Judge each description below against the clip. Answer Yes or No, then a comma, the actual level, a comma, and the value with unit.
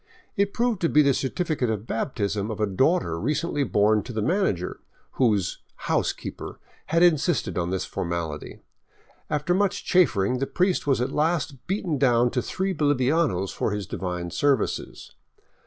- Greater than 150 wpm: Yes, average, 165 wpm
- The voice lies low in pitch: Yes, low, 130 Hz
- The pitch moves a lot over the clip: Yes, wide, 8.3 semitones